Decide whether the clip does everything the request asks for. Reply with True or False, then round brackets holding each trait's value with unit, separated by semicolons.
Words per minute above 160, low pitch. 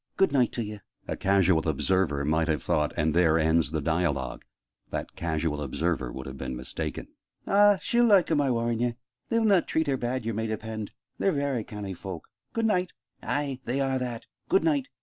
True (190 wpm; 110 Hz)